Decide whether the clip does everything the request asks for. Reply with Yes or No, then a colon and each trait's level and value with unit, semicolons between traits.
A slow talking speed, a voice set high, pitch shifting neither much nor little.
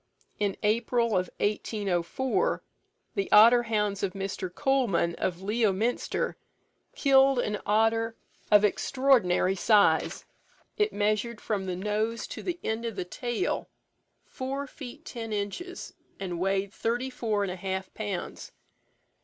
Yes: slow, 125 wpm; high, 215 Hz; average, 3.7 semitones